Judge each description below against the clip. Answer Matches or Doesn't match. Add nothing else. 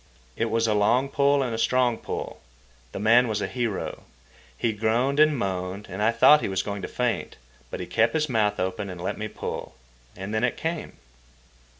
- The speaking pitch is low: Matches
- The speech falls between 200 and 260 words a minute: Matches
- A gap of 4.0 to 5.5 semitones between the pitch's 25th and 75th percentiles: Doesn't match